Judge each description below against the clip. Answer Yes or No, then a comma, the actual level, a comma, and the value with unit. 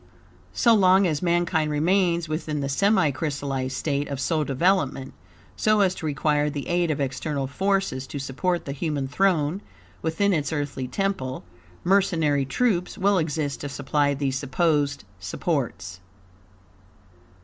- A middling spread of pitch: Yes, average, 4.4 semitones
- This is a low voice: No, medium, 150 Hz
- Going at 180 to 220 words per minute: No, slow, 135 wpm